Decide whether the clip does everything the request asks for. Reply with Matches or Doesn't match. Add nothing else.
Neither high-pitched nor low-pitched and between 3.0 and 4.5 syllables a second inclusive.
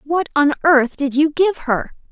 Doesn't match